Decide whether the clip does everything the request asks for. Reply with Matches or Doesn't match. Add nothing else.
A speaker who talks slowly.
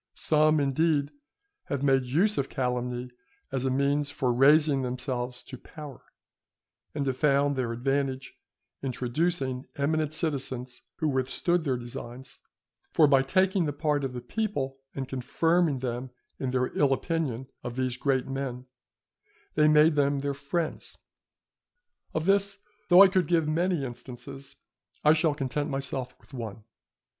Doesn't match